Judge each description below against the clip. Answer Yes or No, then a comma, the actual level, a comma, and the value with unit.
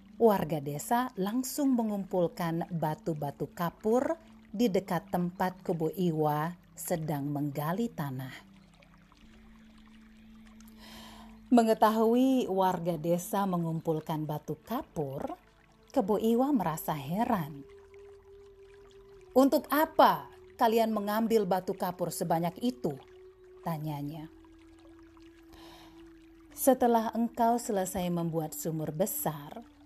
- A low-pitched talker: No, high, 215 Hz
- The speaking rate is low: Yes, slow, 75 wpm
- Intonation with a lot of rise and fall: Yes, wide, 7.0 semitones